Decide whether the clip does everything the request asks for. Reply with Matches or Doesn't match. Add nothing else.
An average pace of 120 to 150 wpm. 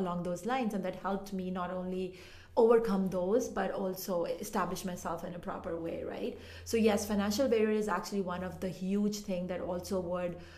Doesn't match